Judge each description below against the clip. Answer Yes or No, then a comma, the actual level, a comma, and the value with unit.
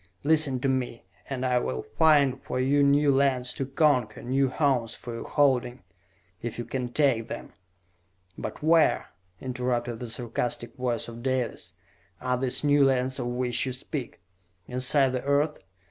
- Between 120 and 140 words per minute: No, average, 160 wpm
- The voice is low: Yes, low, 130 Hz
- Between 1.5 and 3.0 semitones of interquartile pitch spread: Yes, narrow, 2.4 semitones